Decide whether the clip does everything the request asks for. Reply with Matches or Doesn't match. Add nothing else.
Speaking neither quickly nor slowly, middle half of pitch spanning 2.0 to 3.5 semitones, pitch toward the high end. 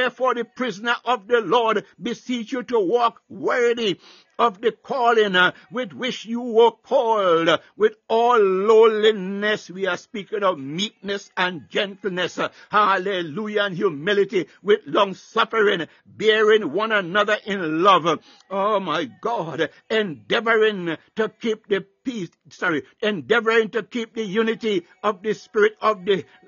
Doesn't match